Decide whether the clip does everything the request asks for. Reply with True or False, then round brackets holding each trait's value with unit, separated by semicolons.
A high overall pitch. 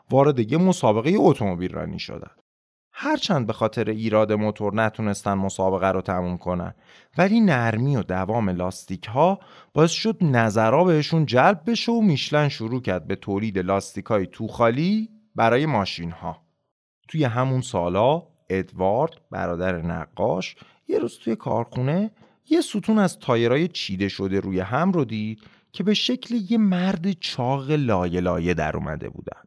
False (115 Hz)